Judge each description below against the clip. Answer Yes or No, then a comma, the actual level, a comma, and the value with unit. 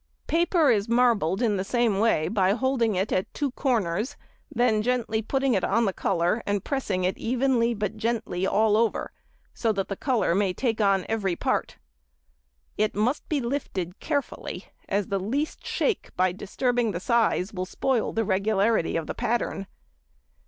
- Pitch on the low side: No, high, 220 Hz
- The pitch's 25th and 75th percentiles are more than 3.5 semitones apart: Yes, average, 4.0 semitones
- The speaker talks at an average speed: Yes, average, 165 wpm